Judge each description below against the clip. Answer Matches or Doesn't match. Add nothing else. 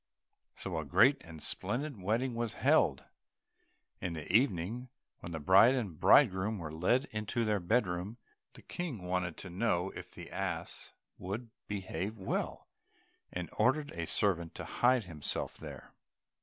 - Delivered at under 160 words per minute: Matches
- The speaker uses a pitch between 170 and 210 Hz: Doesn't match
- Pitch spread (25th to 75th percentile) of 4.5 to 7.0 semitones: Matches